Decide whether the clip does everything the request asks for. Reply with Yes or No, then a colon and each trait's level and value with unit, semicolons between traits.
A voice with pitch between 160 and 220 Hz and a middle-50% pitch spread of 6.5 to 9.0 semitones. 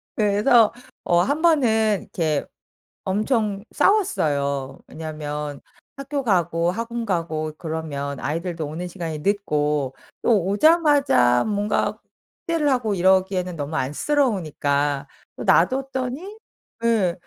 Yes: medium, 185 Hz; wide, 7.4 semitones